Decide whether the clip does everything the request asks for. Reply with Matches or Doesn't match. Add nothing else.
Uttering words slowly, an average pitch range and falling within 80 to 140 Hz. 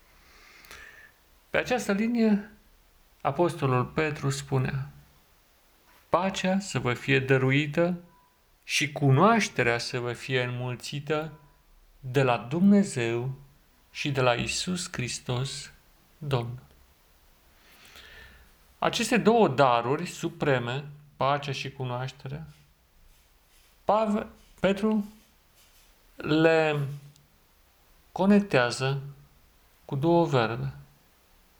Doesn't match